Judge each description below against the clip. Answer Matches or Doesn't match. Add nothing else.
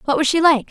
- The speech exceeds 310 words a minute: Matches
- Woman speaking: Matches